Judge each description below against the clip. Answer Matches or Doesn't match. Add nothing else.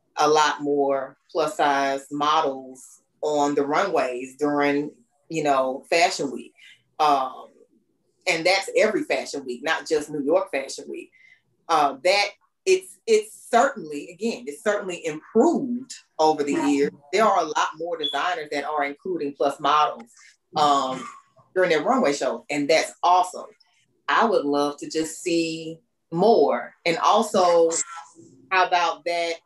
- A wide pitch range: Matches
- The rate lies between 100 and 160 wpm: Matches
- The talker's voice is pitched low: Doesn't match